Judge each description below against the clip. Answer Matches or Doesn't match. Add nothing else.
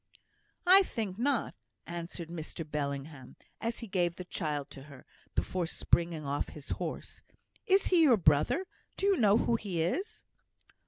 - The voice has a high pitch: Doesn't match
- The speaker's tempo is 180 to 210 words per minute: Doesn't match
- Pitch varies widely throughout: Matches